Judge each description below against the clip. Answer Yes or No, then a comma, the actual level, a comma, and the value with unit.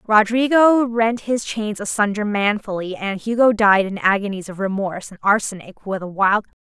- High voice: Yes, high, 210 Hz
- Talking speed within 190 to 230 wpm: No, average, 170 wpm